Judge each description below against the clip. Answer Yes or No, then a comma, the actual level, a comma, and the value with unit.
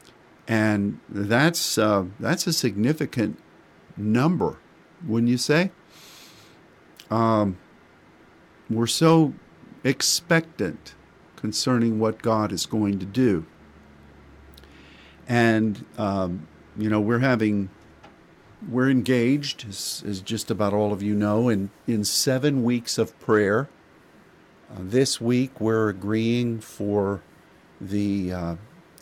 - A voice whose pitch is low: Yes, low, 110 Hz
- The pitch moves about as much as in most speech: Yes, average, 3.9 semitones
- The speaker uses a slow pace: Yes, slow, 105 wpm